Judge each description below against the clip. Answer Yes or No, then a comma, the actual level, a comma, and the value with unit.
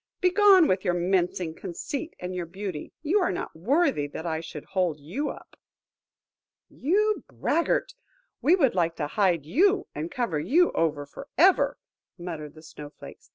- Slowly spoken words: No, average, 160 wpm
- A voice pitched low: No, medium, 185 Hz